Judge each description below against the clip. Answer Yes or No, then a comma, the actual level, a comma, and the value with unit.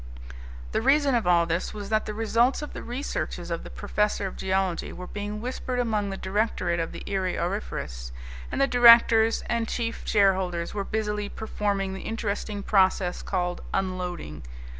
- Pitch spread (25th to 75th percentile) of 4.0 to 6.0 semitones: No, average, 3.4 semitones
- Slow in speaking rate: No, average, 165 wpm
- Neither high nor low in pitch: No, high, 205 Hz